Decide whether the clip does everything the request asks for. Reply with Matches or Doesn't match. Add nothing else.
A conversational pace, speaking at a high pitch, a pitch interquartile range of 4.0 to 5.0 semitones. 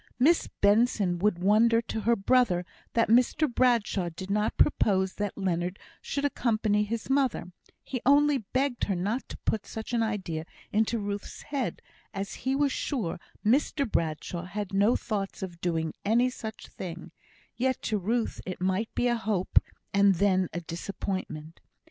Matches